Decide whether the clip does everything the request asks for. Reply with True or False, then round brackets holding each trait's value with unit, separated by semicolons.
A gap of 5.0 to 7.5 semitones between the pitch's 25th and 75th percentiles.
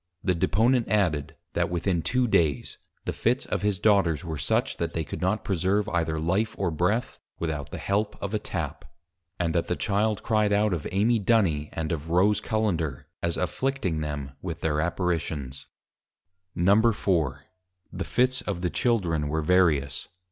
False (4.6 semitones)